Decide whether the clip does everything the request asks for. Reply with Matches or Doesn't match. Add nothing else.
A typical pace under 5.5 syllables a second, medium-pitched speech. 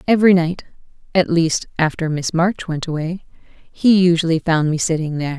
Matches